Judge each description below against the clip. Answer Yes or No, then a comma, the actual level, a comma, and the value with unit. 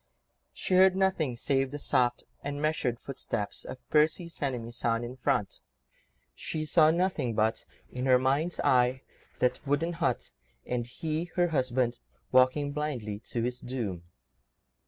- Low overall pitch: Yes, low, 130 Hz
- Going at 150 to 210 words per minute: No, slow, 135 wpm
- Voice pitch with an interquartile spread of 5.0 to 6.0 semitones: No, average, 4.1 semitones